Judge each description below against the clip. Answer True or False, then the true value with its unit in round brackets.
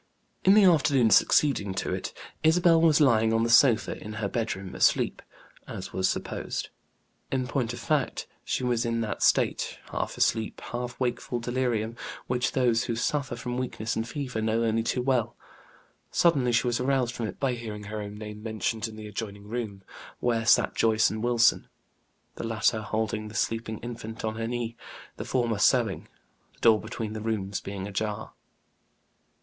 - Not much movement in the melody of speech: True (2.2 semitones)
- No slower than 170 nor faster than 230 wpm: True (175 wpm)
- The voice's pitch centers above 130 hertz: False (115 Hz)